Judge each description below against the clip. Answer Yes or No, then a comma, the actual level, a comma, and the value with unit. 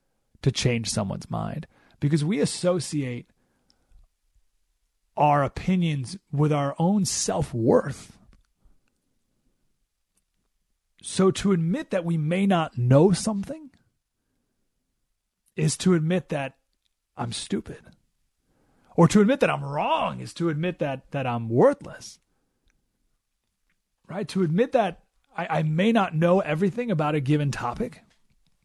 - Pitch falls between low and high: Yes, medium, 165 Hz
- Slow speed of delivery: Yes, slow, 115 wpm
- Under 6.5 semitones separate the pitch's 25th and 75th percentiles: Yes, average, 5.1 semitones